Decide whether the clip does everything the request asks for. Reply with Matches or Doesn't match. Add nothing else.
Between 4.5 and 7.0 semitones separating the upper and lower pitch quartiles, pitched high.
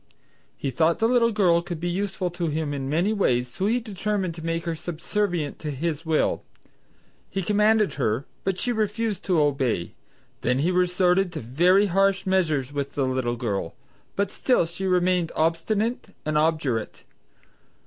Doesn't match